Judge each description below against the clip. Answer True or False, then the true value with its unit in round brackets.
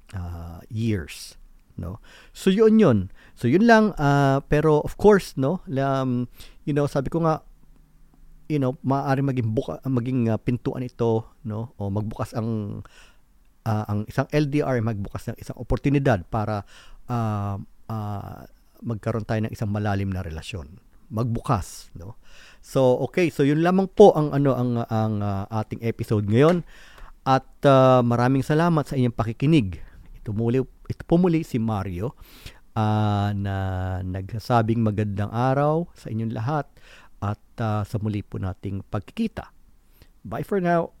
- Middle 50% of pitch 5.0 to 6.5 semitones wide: False (4.5 semitones)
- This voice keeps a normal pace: True (145 wpm)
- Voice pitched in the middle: False (115 Hz)